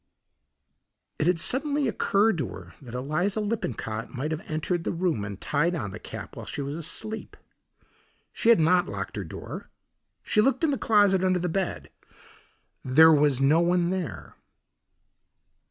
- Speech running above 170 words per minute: No, average, 160 wpm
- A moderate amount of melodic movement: No, wide, 5.7 semitones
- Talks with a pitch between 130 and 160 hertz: No, medium, 170 Hz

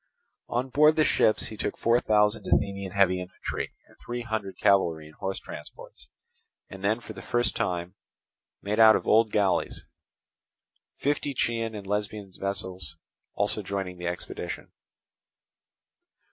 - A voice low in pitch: Yes, low, 100 Hz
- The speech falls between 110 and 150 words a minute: Yes, average, 145 wpm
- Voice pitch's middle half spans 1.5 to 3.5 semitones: Yes, average, 3.1 semitones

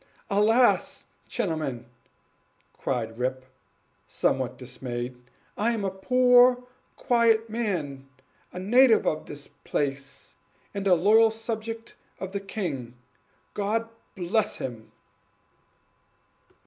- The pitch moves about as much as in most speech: No, wide, 9.0 semitones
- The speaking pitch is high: Yes, high, 195 Hz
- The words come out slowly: Yes, slow, 95 wpm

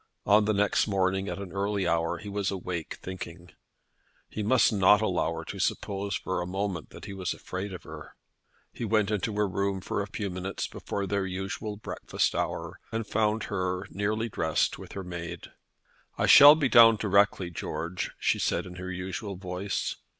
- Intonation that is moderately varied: No, narrow, 2.1 semitones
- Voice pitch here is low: Yes, low, 100 Hz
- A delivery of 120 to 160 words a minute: No, average, 180 wpm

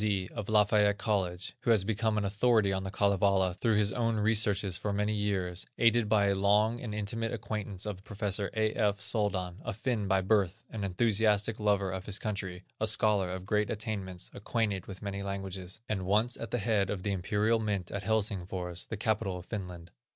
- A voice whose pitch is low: Yes, low, 100 Hz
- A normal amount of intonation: No, narrow, 2.1 semitones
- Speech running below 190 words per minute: No, average, 195 wpm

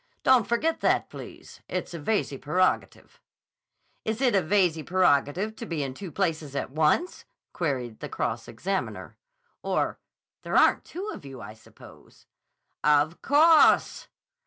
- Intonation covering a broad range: Yes, wide, 7.2 semitones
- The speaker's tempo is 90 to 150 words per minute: Yes, slow, 135 wpm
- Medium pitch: Yes, medium, 175 Hz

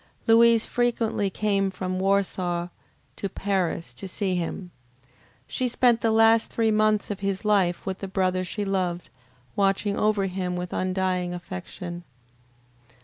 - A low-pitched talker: No, high, 195 Hz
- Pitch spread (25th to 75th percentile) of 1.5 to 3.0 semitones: Yes, average, 2.7 semitones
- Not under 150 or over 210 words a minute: No, average, 140 wpm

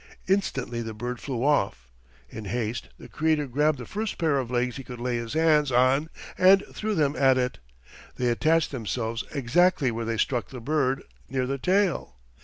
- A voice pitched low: Yes, low, 130 Hz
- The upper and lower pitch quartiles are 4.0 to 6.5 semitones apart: Yes, average, 4.3 semitones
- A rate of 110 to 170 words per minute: No, average, 185 wpm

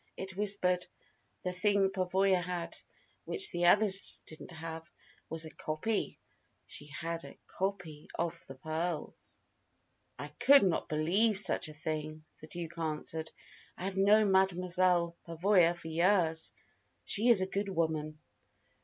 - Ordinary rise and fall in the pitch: Yes, average, 3.2 semitones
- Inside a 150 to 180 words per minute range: No, slow, 135 wpm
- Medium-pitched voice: Yes, medium, 175 Hz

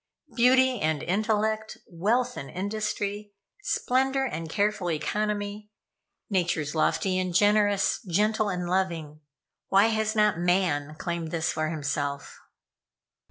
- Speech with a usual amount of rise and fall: Yes, average, 4.4 semitones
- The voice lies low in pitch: No, high, 200 Hz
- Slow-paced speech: Yes, slow, 115 wpm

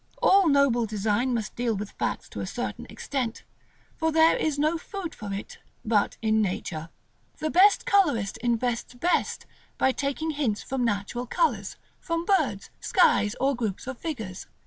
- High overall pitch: Yes, very high, 250 Hz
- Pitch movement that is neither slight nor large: No, wide, 6.5 semitones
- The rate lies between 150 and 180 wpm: Yes, average, 160 wpm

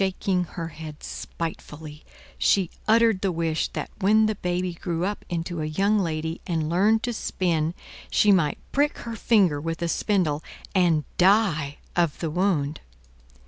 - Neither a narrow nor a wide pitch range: Yes, average, 3.8 semitones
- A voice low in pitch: No, medium, 175 Hz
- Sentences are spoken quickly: No, average, 155 wpm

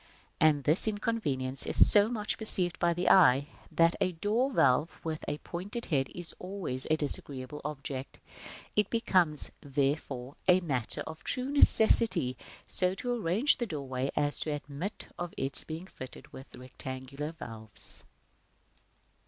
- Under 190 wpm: Yes, average, 145 wpm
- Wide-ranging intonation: Yes, wide, 5.9 semitones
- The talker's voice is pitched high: No, medium, 155 Hz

